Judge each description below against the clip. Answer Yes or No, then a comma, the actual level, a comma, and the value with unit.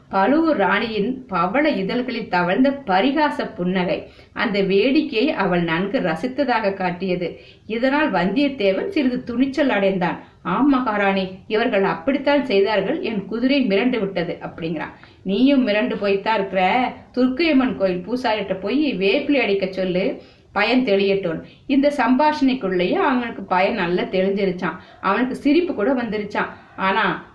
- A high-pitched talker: Yes, high, 215 Hz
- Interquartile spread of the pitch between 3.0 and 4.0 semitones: No, wide, 5.4 semitones